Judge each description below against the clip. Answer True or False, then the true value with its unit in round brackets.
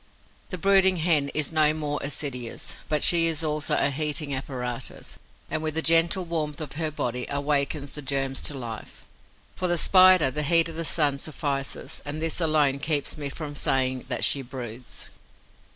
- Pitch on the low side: False (150 Hz)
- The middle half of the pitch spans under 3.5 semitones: True (2.8 semitones)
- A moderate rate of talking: True (175 wpm)